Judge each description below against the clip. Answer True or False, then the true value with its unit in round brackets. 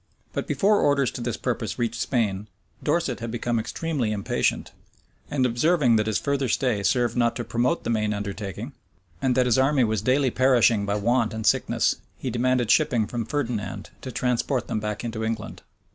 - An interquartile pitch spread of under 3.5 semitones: True (3.0 semitones)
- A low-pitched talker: True (120 Hz)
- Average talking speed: True (180 wpm)